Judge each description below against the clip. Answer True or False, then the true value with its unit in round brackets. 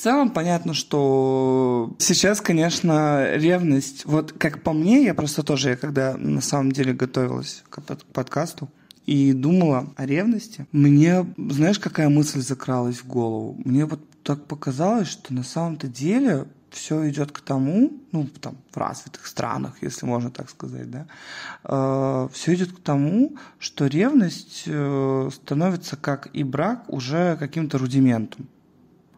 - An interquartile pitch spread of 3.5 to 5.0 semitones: True (4.0 semitones)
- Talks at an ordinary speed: True (140 wpm)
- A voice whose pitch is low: False (145 Hz)